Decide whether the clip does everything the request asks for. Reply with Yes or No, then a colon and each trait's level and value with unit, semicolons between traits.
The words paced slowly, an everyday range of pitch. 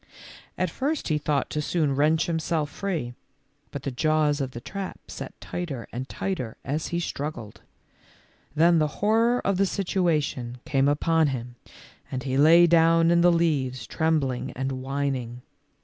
No: average, 155 wpm; average, 4.3 semitones